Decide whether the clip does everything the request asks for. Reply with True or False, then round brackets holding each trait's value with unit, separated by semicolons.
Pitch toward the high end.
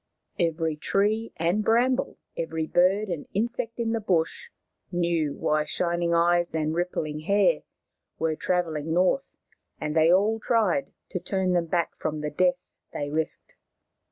False (175 Hz)